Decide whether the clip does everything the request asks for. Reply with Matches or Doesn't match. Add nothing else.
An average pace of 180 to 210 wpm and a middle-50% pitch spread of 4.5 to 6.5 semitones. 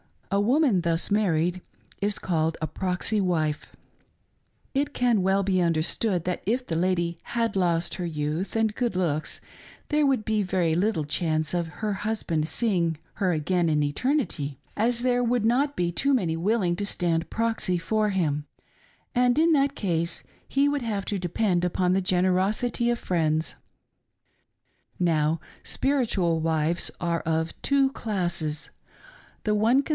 Doesn't match